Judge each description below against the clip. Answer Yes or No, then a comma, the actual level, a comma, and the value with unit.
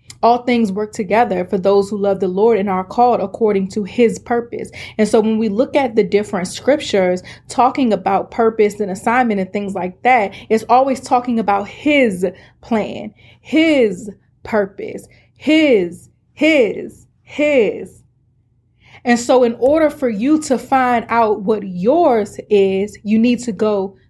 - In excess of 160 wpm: No, average, 155 wpm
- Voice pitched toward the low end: No, high, 220 Hz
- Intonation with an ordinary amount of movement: Yes, average, 3.8 semitones